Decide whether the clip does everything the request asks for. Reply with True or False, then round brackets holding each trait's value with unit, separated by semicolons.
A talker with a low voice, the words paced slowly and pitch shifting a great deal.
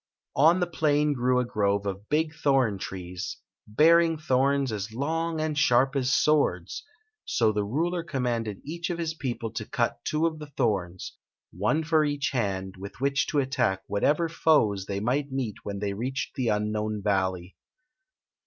False (130 Hz; 170 wpm; 6.6 semitones)